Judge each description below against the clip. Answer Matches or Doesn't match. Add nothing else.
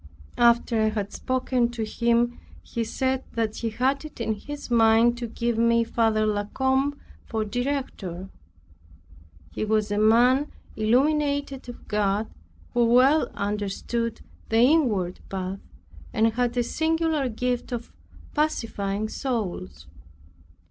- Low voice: Doesn't match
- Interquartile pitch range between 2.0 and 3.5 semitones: Matches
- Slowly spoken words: Matches